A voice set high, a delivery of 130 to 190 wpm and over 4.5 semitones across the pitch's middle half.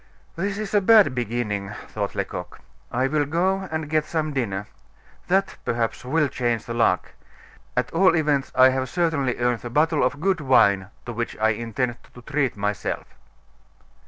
No: low, 130 Hz; average, 165 wpm; wide, 5.4 semitones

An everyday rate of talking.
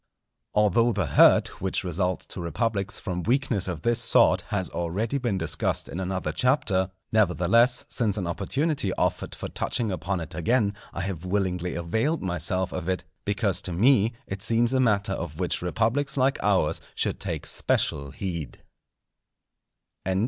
Yes: average, 155 wpm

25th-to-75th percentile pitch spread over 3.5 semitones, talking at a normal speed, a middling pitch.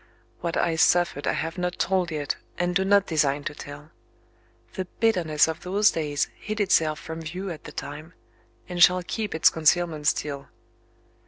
No: average, 3.1 semitones; average, 170 wpm; medium, 165 Hz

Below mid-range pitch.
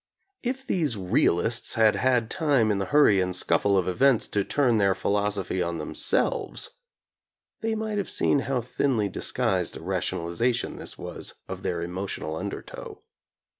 Yes: low, 110 Hz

